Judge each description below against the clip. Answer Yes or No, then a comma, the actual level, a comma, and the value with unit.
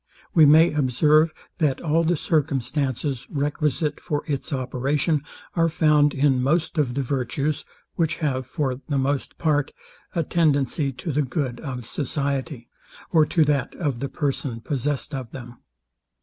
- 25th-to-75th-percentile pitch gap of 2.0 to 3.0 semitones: Yes, narrow, 2.6 semitones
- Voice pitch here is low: No, medium, 145 Hz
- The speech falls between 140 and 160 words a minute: Yes, average, 150 wpm